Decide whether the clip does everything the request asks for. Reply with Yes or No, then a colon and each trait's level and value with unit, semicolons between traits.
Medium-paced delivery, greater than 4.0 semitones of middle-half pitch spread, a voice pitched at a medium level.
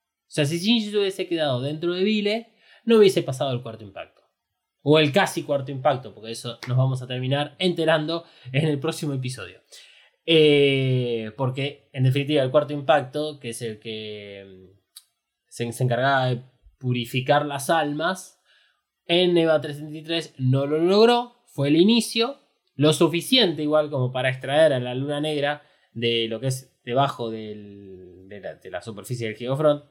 Yes: average, 160 wpm; average, 4.5 semitones; medium, 145 Hz